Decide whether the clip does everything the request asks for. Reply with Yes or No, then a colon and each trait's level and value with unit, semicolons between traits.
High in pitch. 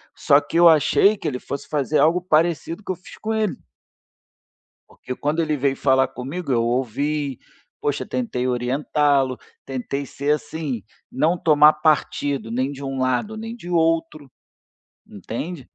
No: medium, 145 Hz